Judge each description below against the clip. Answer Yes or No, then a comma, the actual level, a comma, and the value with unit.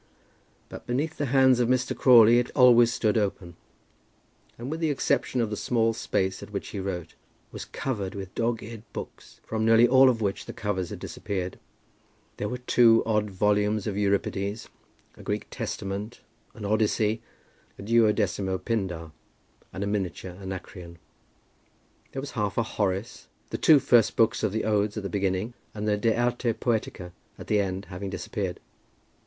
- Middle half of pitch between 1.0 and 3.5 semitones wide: Yes, average, 3.2 semitones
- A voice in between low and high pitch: No, low, 105 Hz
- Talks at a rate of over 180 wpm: No, average, 170 wpm